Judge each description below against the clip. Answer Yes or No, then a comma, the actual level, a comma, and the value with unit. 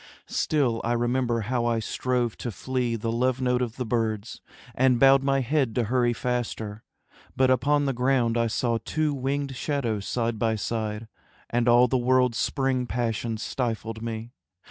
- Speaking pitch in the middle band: No, low, 120 Hz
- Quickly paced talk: No, average, 165 wpm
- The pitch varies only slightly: Yes, narrow, 2.1 semitones